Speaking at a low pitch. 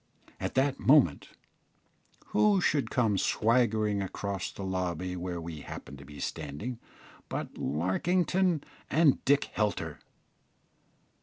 Yes: low, 105 Hz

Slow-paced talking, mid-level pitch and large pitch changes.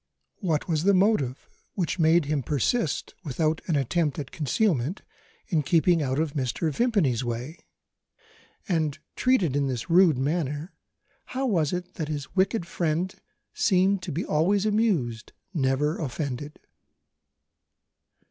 No: slow, 130 wpm; medium, 160 Hz; average, 4.6 semitones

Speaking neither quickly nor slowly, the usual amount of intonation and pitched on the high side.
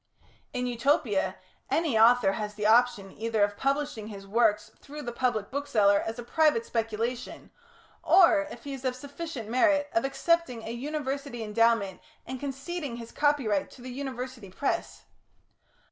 Yes: average, 150 wpm; average, 4.3 semitones; high, 245 Hz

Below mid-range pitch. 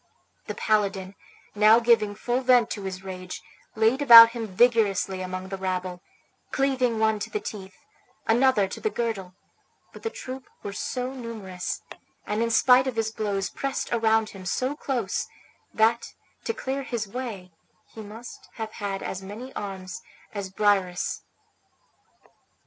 No: high, 220 Hz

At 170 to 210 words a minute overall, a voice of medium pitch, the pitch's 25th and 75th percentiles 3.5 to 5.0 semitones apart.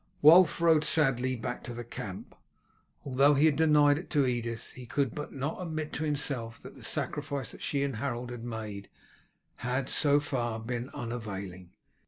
No: average, 175 wpm; low, 130 Hz; average, 3.8 semitones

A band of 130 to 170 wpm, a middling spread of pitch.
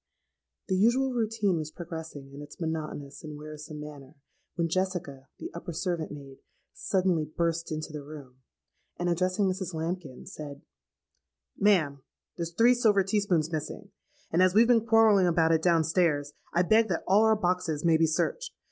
Yes: average, 165 wpm; average, 3.8 semitones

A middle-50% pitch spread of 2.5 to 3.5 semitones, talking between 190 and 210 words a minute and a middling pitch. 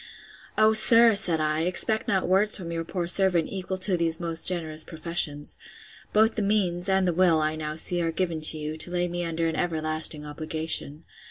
Yes: average, 2.9 semitones; average, 195 wpm; medium, 170 Hz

